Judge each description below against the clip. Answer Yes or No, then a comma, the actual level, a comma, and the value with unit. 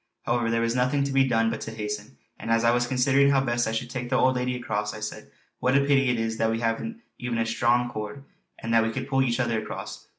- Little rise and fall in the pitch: Yes, narrow, 2.3 semitones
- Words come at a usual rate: No, fast, 270 wpm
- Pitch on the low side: Yes, low, 120 Hz